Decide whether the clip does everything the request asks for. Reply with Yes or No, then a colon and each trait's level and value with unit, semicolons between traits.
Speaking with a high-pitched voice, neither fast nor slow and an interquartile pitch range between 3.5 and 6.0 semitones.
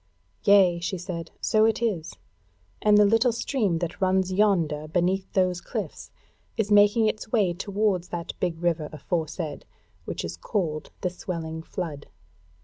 No: medium, 180 Hz; average, 145 wpm; average, 3.9 semitones